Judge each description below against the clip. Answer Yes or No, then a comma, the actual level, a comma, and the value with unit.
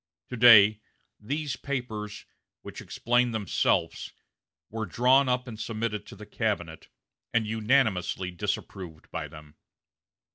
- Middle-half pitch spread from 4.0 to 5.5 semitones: No, average, 3.6 semitones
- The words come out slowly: Yes, slow, 115 wpm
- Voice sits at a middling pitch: No, low, 110 Hz